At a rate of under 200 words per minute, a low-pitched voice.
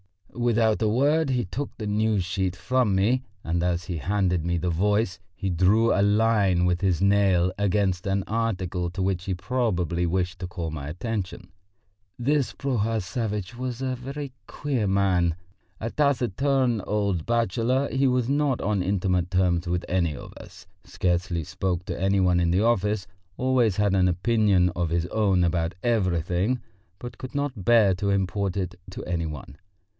Yes: average, 170 wpm; low, 100 Hz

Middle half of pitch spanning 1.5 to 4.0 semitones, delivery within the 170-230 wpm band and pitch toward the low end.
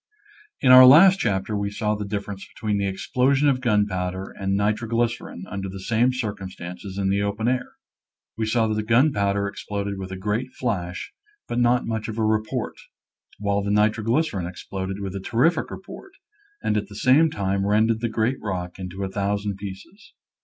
Yes: average, 3.2 semitones; average, 180 wpm; low, 105 Hz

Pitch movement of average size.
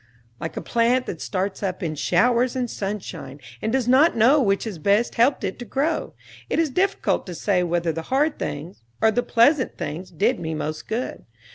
No: wide, 6.5 semitones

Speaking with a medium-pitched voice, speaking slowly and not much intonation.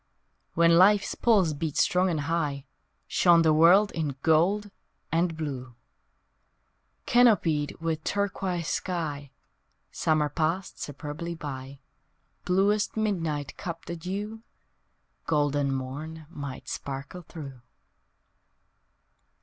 No: medium, 165 Hz; slow, 100 wpm; average, 3.8 semitones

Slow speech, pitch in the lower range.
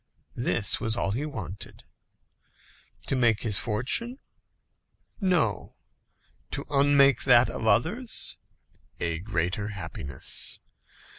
Yes: slow, 95 wpm; low, 115 Hz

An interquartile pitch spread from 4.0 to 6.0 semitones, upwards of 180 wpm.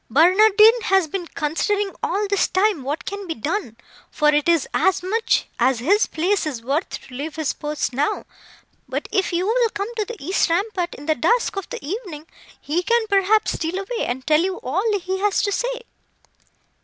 Yes: average, 5.2 semitones; average, 190 wpm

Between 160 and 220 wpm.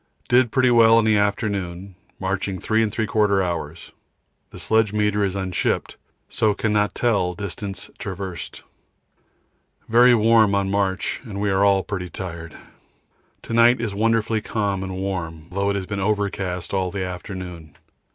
No: average, 150 wpm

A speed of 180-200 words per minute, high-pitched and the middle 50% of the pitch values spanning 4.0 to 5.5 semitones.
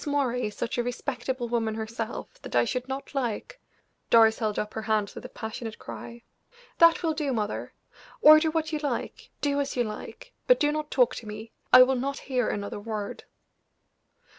Yes: average, 190 wpm; high, 245 Hz; average, 4.4 semitones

